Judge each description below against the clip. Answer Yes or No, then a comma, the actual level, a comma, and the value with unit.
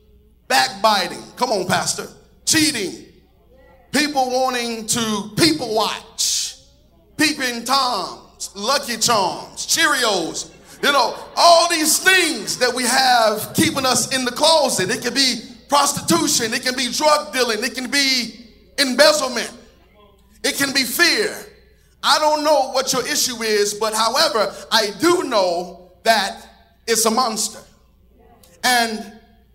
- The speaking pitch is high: Yes, very high, 255 Hz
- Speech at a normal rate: No, slow, 125 wpm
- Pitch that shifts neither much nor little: Yes, average, 4.2 semitones